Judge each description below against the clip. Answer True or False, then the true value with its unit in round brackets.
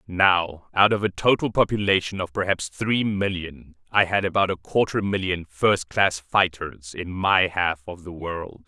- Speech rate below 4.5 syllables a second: True (4.2 syllables/s)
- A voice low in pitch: True (95 Hz)